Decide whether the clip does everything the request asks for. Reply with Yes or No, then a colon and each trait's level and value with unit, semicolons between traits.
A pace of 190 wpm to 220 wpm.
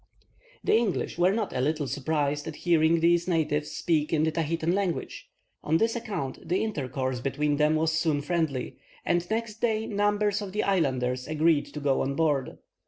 No: average, 175 wpm